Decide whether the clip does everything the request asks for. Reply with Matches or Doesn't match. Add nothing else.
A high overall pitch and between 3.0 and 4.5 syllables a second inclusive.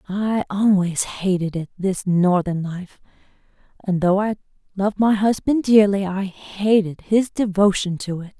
Matches